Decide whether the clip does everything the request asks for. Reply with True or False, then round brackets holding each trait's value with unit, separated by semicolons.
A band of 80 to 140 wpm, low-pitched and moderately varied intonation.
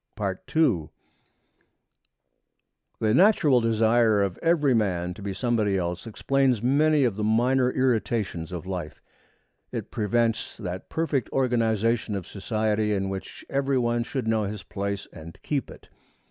True (135 wpm; 110 Hz; 4.3 semitones)